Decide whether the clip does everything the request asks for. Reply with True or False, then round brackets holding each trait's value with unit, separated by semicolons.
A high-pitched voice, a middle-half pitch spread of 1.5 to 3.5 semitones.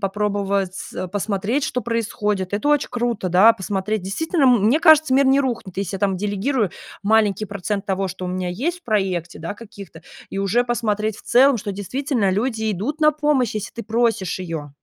False (210 Hz; 4.0 semitones)